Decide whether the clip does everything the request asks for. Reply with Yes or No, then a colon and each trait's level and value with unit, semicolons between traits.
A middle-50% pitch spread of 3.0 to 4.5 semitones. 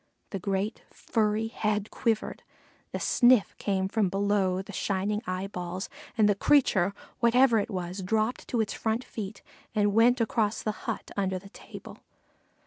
No: narrow, 2.5 semitones